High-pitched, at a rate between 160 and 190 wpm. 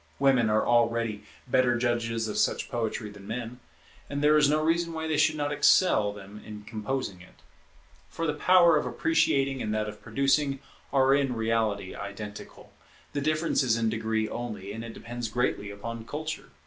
No: low, 120 Hz; average, 175 wpm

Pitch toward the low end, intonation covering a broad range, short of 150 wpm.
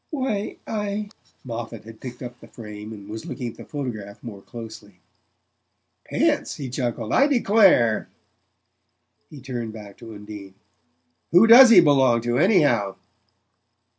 Yes: low, 120 Hz; wide, 8.2 semitones; average, 140 wpm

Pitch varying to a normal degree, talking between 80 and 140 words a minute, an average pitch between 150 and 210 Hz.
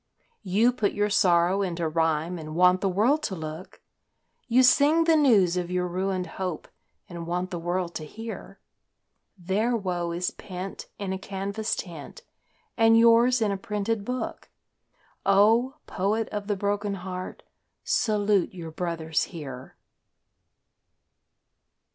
Yes: average, 3.7 semitones; slow, 135 wpm; high, 190 Hz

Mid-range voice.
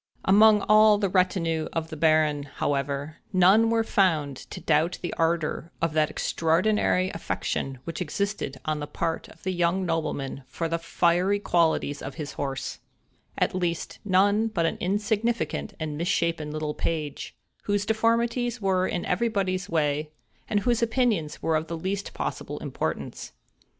Yes: medium, 170 Hz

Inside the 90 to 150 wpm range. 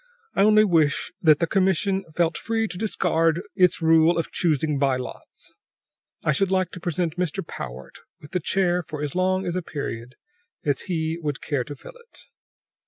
No: average, 175 wpm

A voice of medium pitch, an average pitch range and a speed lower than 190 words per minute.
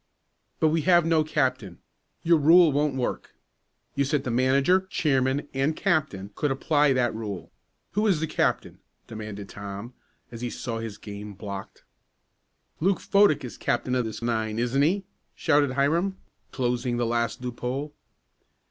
No: low, 130 Hz; average, 5.0 semitones; average, 150 wpm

